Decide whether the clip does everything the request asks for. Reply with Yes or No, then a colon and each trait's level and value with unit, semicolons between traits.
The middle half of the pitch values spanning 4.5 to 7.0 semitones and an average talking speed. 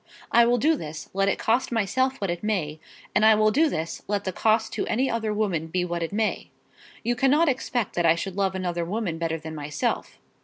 No: average, 5.2 semitones; fast, 225 wpm